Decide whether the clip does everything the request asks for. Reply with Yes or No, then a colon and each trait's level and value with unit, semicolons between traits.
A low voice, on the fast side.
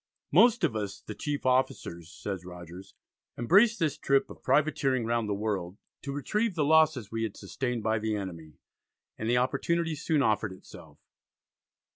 No: low, 125 Hz; average, 160 wpm